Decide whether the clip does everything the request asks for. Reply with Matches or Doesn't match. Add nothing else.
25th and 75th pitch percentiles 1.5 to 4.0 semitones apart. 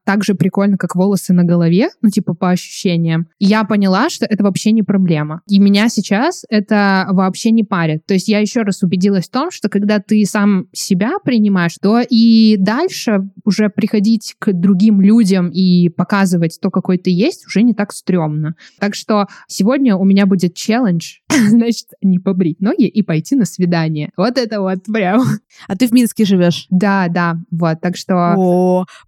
Matches